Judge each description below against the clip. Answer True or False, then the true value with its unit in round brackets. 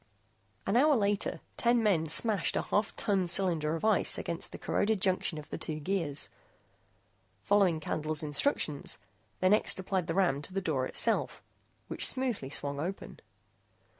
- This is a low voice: False (185 Hz)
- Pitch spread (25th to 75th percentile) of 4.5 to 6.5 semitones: True (4.8 semitones)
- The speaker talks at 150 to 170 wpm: True (155 wpm)